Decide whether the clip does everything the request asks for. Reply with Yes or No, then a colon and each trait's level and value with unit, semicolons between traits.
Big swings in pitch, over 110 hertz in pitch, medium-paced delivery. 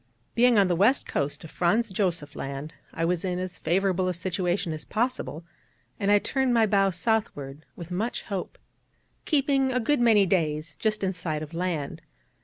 No: average, 4.9 semitones; medium, 185 Hz; average, 180 wpm